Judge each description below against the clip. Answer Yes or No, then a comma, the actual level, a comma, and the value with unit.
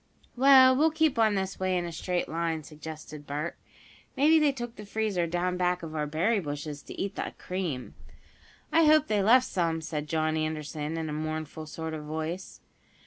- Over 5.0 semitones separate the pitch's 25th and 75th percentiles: Yes, wide, 5.6 semitones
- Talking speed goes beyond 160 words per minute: Yes, average, 190 wpm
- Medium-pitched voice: Yes, medium, 170 Hz